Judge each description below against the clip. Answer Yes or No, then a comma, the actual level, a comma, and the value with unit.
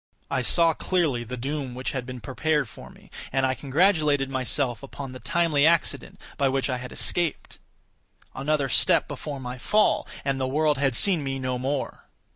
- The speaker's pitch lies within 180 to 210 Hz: No, low, 135 Hz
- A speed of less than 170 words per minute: No, average, 175 wpm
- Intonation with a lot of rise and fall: No, average, 2.9 semitones